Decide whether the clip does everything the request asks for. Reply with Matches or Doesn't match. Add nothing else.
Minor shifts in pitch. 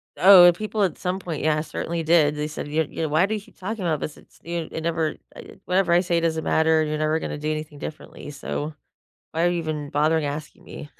Matches